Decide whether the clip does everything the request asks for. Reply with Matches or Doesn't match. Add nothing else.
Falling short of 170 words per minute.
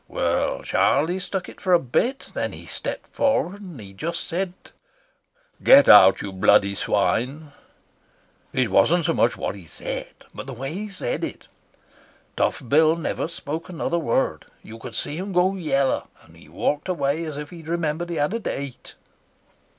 Doesn't match